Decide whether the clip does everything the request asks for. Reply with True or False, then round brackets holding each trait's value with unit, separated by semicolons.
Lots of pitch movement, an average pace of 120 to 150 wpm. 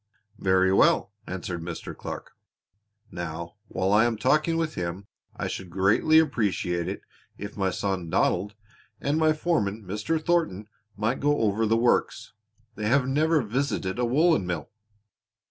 True (7.1 semitones; 145 wpm)